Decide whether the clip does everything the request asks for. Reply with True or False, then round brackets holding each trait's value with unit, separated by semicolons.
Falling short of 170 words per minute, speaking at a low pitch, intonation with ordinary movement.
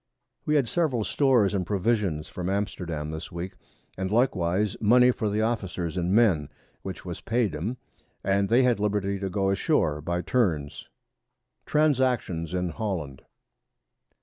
True (150 wpm; 100 Hz; 5.0 semitones)